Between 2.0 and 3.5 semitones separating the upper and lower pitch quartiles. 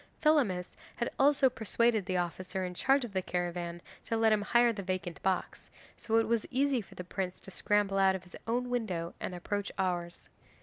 No: average, 4.5 semitones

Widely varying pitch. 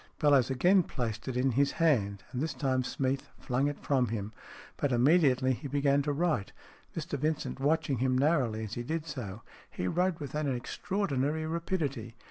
No: average, 3.8 semitones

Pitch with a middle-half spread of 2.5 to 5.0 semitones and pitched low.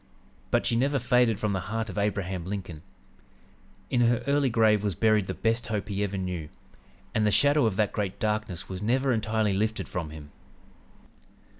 Yes: average, 3.1 semitones; low, 105 Hz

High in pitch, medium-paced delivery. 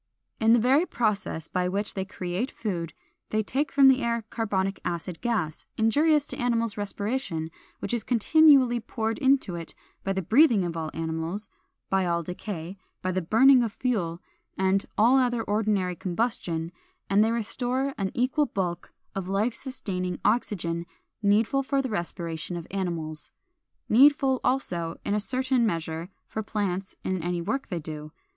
Yes: high, 205 Hz; average, 160 wpm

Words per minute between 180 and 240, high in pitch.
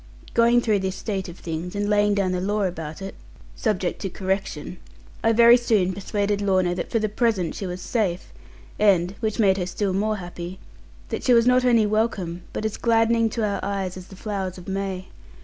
Yes: average, 200 wpm; high, 200 Hz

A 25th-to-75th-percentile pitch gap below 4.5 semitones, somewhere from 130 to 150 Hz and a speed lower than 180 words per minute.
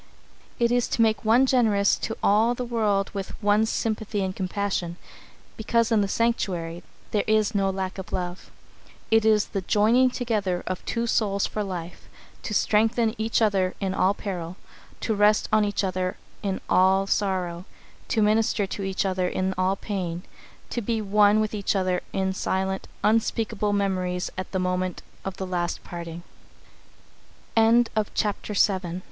No: average, 2.8 semitones; high, 200 Hz; average, 145 wpm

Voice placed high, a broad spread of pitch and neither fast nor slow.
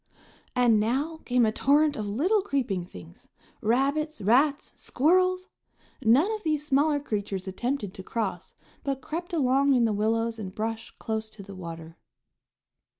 Yes: high, 245 Hz; wide, 5.8 semitones; average, 150 wpm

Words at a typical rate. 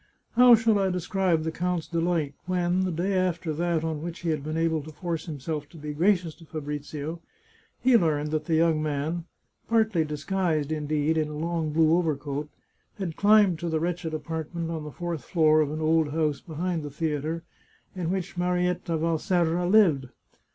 Yes: average, 185 wpm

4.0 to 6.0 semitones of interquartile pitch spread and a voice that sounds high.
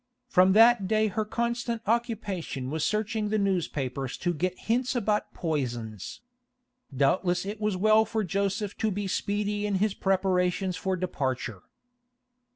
No: average, 3.6 semitones; high, 195 Hz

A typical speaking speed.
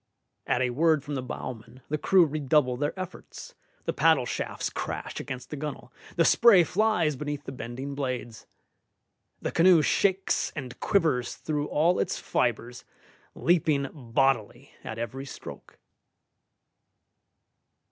No: slow, 130 wpm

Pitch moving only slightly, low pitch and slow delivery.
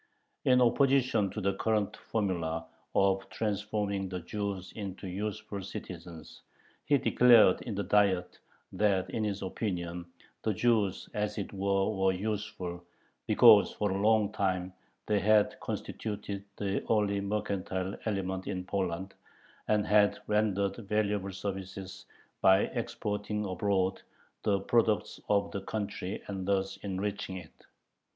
Yes: narrow, 1.9 semitones; low, 100 Hz; slow, 130 wpm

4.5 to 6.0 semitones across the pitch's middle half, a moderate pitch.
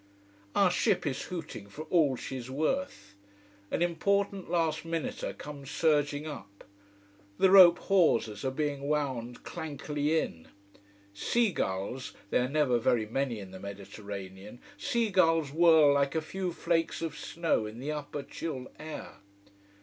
Yes: average, 5.2 semitones; medium, 150 Hz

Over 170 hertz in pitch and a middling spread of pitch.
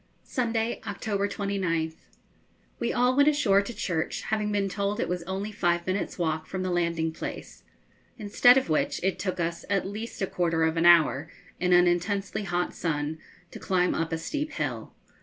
Yes: medium, 185 Hz; average, 3.5 semitones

